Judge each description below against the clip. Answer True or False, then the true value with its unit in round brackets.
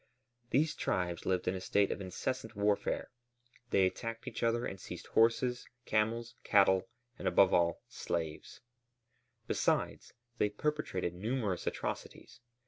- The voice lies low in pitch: True (105 Hz)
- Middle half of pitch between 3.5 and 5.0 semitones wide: True (4.1 semitones)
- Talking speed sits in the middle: False (130 wpm)